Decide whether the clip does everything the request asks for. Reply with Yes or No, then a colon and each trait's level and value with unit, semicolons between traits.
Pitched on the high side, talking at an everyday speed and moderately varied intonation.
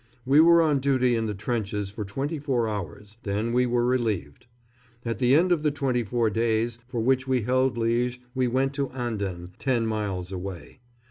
No: low, 120 Hz; average, 190 wpm; average, 3.5 semitones